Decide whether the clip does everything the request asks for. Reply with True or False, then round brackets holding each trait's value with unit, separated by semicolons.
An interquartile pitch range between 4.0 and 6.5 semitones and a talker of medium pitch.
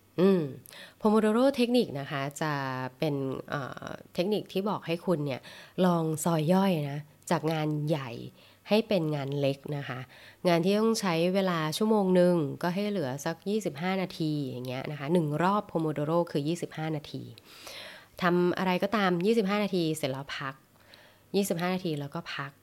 True (4.6 semitones; 170 Hz)